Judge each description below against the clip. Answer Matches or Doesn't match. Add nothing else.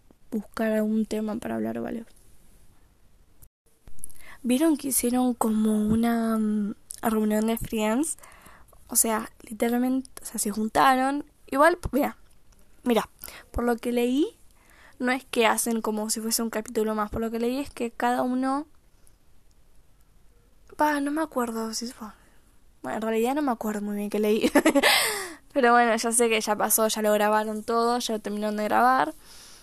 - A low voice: Doesn't match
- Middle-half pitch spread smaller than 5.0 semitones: Matches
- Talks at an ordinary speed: Matches